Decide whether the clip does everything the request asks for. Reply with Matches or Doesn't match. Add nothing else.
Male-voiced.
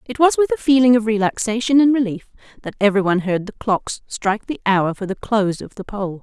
Doesn't match